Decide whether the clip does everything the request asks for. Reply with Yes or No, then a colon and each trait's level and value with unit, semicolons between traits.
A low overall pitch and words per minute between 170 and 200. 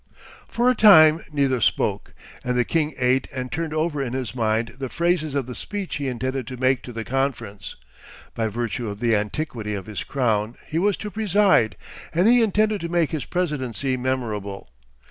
Yes: low, 130 Hz; average, 185 wpm